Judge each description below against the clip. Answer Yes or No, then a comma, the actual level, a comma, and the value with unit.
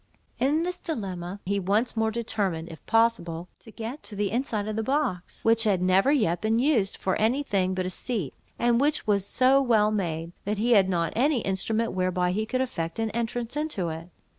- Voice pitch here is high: Yes, high, 215 Hz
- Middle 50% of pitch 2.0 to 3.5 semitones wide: No, average, 4.4 semitones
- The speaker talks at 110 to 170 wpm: No, fast, 205 wpm